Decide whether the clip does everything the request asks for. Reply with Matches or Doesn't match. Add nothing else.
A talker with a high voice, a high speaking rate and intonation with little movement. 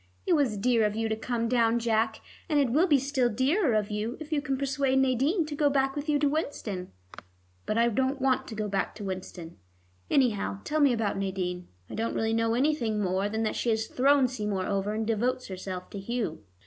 Doesn't match